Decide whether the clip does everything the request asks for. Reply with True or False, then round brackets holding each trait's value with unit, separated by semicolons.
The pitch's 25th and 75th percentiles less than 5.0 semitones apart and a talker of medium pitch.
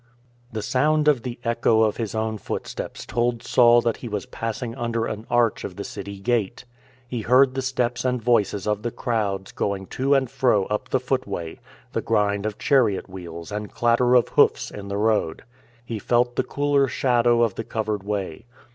False (3.0 semitones; 115 Hz)